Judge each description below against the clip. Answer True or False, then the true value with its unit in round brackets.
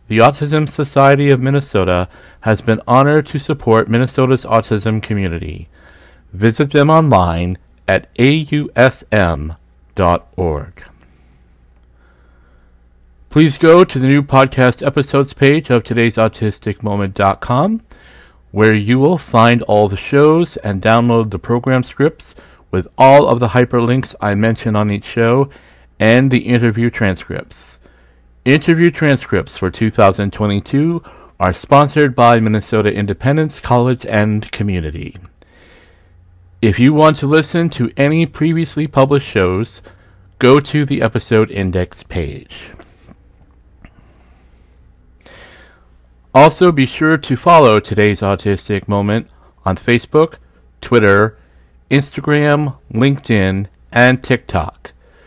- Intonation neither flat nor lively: False (7.2 semitones)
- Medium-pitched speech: False (110 Hz)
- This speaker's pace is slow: True (105 wpm)